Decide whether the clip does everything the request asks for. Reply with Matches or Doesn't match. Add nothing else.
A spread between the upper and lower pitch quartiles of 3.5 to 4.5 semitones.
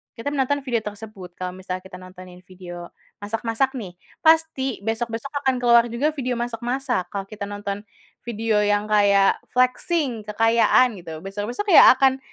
Matches